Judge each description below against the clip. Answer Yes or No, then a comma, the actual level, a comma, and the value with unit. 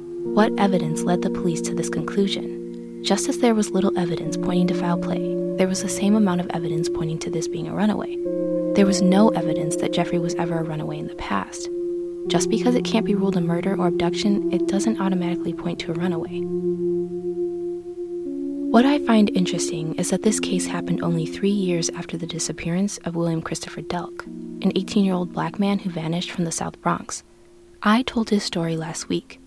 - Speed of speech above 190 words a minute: Yes, average, 200 wpm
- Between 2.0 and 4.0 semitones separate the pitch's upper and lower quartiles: Yes, narrow, 2.4 semitones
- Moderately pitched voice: Yes, medium, 175 Hz